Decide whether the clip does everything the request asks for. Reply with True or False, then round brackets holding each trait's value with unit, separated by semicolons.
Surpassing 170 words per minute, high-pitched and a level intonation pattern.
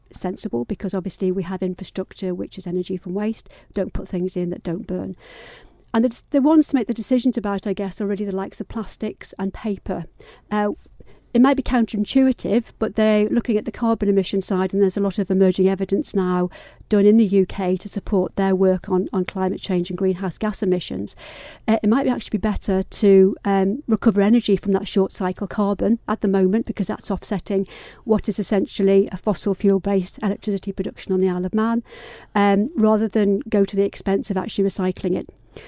True (200 wpm; 200 Hz; 2.3 semitones)